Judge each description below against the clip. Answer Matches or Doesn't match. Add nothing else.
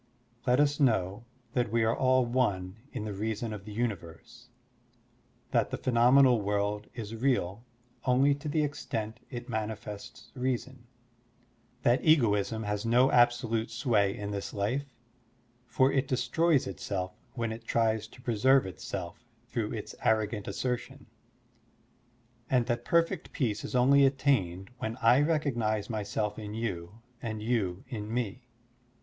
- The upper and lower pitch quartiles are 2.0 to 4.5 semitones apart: Matches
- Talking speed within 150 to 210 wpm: Doesn't match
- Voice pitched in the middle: Doesn't match